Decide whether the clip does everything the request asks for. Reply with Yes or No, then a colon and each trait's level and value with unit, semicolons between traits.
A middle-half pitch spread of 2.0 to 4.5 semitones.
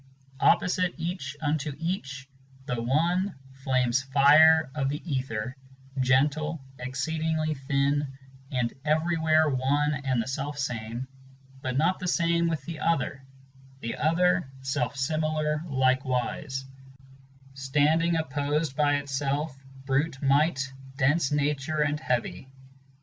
Yes: average, 3.0 semitones